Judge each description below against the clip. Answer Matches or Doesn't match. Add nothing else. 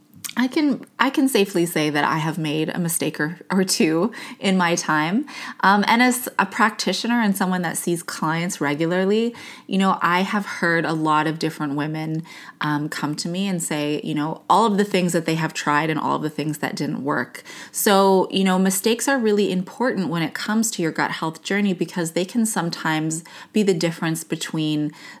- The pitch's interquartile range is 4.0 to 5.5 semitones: Matches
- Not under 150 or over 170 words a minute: Doesn't match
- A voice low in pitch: Doesn't match